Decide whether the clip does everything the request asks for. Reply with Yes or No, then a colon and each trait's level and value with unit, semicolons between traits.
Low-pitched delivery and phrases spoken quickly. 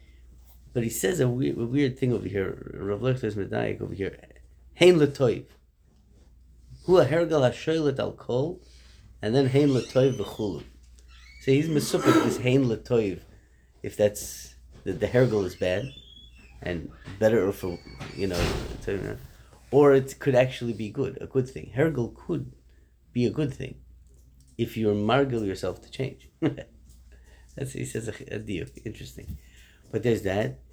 No: low, 105 Hz; slow, 135 wpm